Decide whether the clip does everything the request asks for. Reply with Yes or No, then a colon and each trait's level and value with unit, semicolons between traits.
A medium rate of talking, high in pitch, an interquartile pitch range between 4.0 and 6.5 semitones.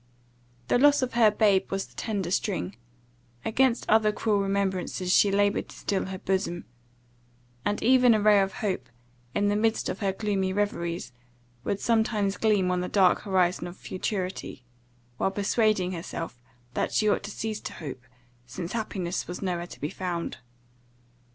No: average, 165 wpm; high, 195 Hz; average, 2.7 semitones